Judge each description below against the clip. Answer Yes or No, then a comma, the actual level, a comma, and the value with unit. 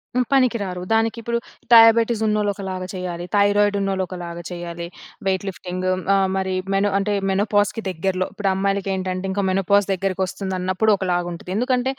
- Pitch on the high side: Yes, high, 195 Hz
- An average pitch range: No, narrow, 2.1 semitones